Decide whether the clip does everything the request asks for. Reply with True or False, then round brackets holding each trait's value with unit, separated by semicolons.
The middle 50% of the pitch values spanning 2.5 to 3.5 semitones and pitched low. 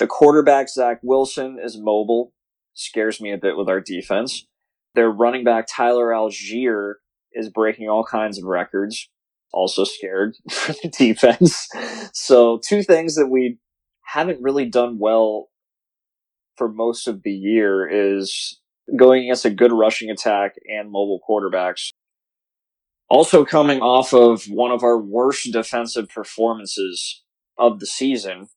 True (3.1 semitones; 115 Hz)